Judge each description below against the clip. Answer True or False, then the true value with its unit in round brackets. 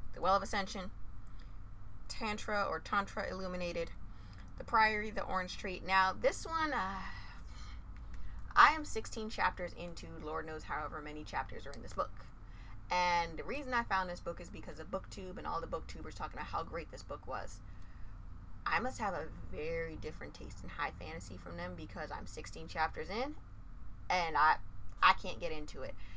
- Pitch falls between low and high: True (175 Hz)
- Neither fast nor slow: True (175 wpm)